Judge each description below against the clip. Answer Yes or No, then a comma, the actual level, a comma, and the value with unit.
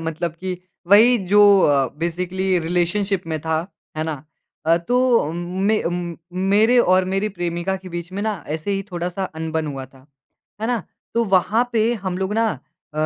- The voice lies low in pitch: No, medium, 180 Hz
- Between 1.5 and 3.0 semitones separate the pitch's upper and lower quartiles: No, average, 3.5 semitones